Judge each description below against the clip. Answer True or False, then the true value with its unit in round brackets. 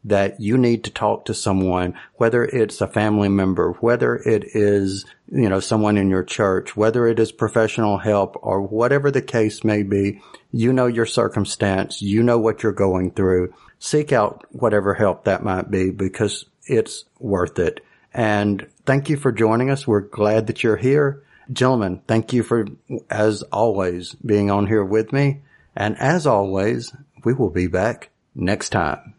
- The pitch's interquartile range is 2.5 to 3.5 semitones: True (3.2 semitones)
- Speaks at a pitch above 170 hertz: False (105 Hz)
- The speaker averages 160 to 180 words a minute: True (175 wpm)